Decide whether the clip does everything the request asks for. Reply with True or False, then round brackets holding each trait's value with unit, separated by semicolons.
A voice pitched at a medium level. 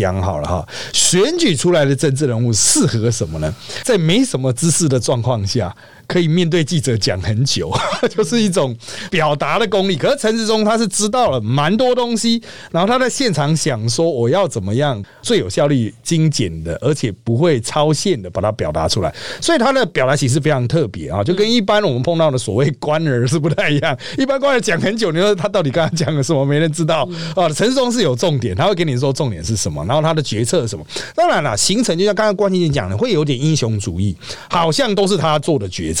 True (155 Hz)